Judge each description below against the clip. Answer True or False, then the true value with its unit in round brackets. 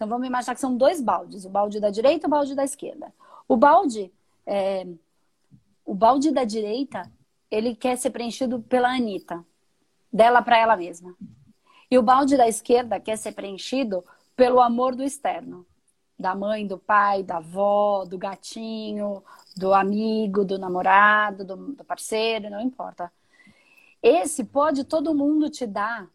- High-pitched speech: True (220 Hz)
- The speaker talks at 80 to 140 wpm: False (155 wpm)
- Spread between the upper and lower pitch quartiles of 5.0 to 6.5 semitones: False (4.5 semitones)